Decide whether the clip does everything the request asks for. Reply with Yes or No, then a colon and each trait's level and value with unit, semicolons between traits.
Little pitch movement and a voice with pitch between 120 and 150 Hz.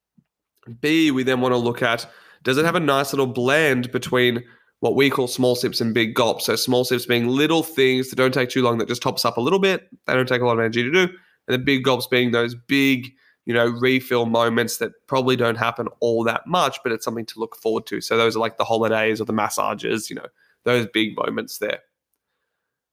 Yes: narrow, 2.0 semitones; low, 125 Hz